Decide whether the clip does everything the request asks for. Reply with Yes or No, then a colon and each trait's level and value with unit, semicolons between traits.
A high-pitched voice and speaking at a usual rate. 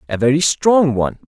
No: medium, 140 Hz; average, 185 wpm